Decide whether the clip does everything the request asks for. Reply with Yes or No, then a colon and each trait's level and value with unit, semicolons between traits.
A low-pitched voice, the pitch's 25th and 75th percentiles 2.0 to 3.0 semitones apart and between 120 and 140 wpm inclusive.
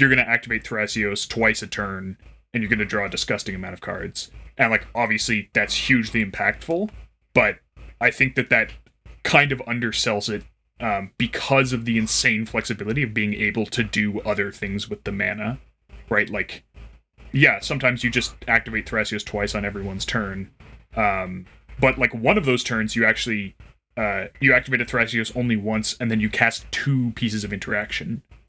No: low, 110 Hz; narrow, 2.4 semitones; average, 180 wpm